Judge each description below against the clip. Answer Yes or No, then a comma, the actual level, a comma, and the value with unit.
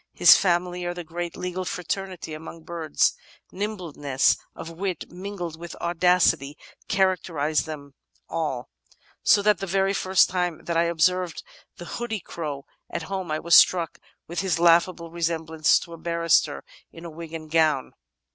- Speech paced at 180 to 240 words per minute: No, average, 150 wpm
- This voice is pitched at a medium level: Yes, medium, 170 Hz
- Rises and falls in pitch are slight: Yes, narrow, 2.1 semitones